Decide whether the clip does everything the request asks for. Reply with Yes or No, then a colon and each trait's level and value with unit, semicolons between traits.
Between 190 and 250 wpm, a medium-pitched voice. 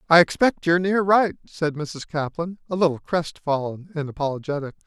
No: average, 160 wpm; medium, 160 Hz